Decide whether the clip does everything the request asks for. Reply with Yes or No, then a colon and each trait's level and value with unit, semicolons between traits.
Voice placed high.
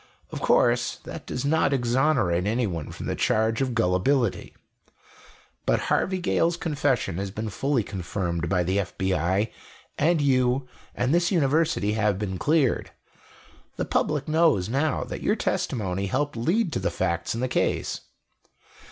No: low, 120 Hz